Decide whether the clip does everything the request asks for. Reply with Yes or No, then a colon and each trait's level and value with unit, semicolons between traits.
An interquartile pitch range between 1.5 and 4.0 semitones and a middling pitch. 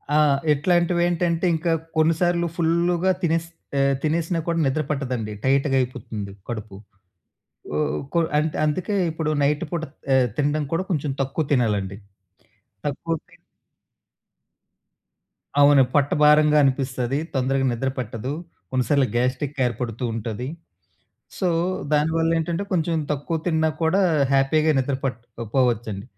No: average, 4.4 semitones; medium, 145 Hz